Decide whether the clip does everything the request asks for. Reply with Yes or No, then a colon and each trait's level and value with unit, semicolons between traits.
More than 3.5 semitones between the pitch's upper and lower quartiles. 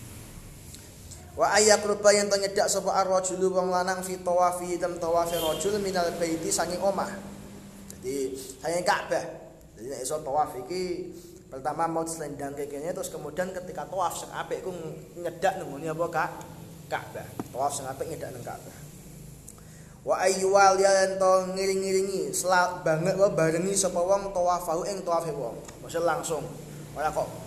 No: average, 2.9 semitones